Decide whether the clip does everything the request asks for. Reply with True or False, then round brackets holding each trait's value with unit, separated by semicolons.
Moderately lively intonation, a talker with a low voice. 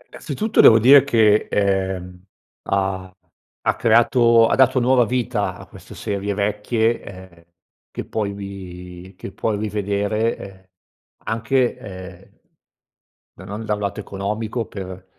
True (3.1 semitones; 105 Hz)